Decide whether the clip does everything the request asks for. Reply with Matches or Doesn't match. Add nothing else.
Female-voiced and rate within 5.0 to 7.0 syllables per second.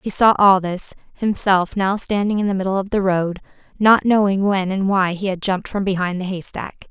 Matches